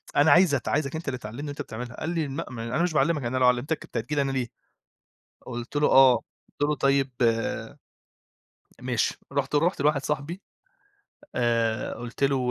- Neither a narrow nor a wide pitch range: Yes, average, 3.3 semitones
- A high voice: No, medium, 140 Hz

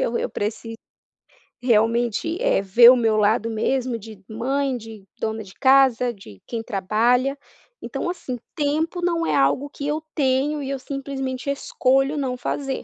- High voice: Yes, very high, 255 Hz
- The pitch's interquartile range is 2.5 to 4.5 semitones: Yes, average, 3.7 semitones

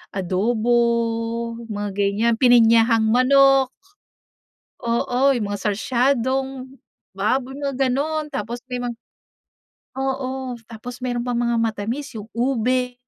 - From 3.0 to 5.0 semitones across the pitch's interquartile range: No, narrow, 2.5 semitones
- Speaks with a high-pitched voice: Yes, high, 240 Hz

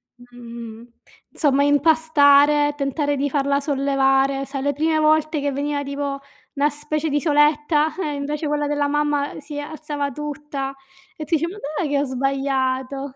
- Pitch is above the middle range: Yes, very high, 285 Hz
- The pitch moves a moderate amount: No, narrow, 1.4 semitones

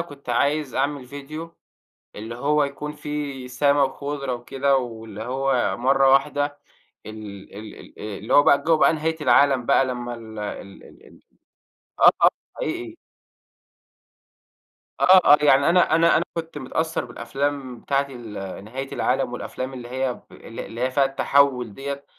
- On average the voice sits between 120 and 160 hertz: Yes, low, 135 Hz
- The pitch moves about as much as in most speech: Yes, average, 3.0 semitones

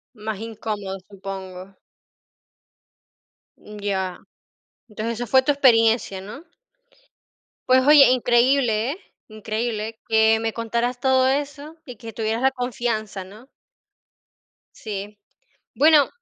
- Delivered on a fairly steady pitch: No, average, 3.5 semitones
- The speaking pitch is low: No, high, 225 Hz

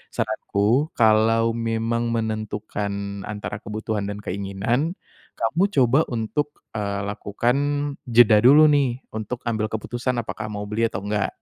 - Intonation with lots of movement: No, average, 2.7 semitones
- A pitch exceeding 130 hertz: No, low, 110 Hz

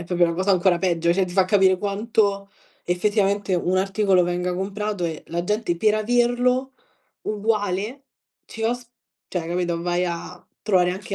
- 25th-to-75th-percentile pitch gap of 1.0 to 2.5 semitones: No, average, 2.9 semitones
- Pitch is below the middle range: No, high, 190 Hz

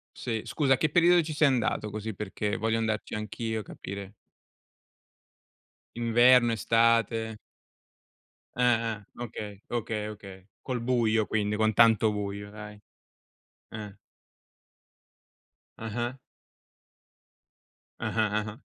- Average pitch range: No, narrow, 2.0 semitones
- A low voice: Yes, low, 110 Hz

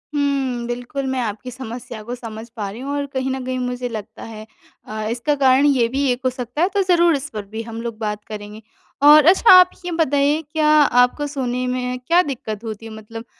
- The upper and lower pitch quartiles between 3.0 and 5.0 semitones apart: Yes, average, 4.0 semitones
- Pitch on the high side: Yes, very high, 250 Hz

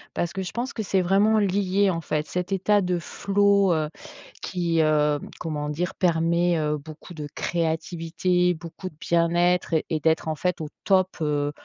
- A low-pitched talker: No, medium, 175 Hz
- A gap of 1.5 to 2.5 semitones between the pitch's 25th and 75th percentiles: No, average, 2.9 semitones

